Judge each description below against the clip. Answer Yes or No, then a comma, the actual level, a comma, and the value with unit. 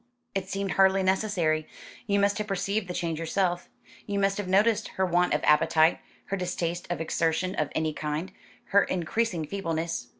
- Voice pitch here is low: No, medium, 185 Hz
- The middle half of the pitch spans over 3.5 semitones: No, average, 3.1 semitones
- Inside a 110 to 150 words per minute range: No, average, 170 wpm